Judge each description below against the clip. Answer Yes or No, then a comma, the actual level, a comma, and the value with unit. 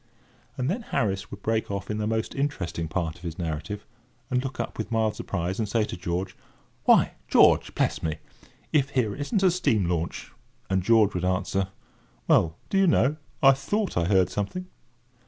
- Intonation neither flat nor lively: No, wide, 6.5 semitones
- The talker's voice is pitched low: Yes, low, 105 Hz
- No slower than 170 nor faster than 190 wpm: Yes, average, 185 wpm